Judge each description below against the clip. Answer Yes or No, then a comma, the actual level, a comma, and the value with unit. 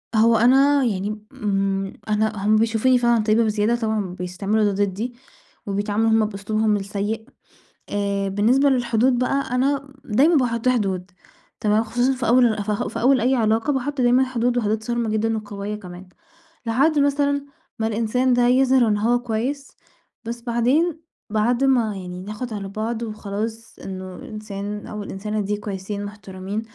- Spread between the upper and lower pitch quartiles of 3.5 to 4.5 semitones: No, average, 3.1 semitones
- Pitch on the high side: Yes, high, 220 Hz